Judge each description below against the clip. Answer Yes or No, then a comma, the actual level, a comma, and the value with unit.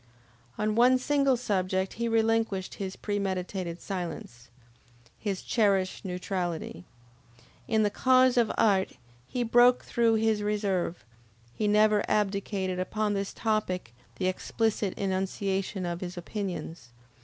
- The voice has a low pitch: No, high, 200 Hz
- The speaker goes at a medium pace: No, slow, 120 wpm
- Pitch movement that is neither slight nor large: Yes, average, 3.0 semitones